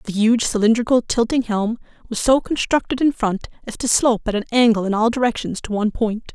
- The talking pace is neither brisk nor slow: No, fast, 210 wpm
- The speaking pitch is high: Yes, high, 230 Hz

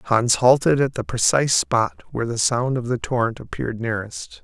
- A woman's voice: No, male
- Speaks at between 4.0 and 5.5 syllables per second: Yes, 5.4 syllables/s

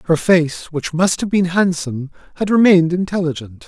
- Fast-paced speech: No, average, 165 wpm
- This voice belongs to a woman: No, male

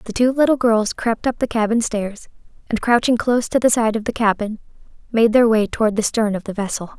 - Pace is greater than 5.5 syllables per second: Yes, 5.7 syllables/s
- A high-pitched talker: Yes, high, 225 Hz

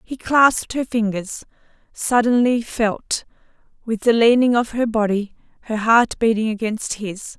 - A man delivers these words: No, female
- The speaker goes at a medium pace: No, slow, 130 wpm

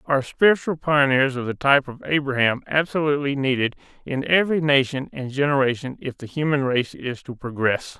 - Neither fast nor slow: Yes, average, 165 wpm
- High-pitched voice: No, low, 135 Hz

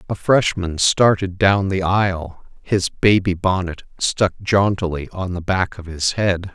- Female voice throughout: No, male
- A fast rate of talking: No, average, 155 wpm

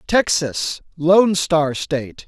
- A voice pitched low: No, medium, 160 Hz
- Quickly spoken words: No, slow, 105 wpm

